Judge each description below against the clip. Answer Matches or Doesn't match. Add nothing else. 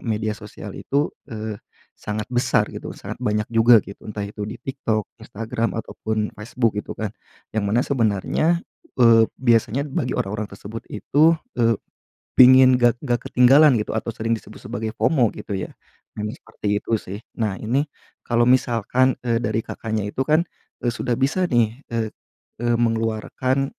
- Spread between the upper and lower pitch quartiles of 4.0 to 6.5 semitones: Doesn't match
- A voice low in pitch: Matches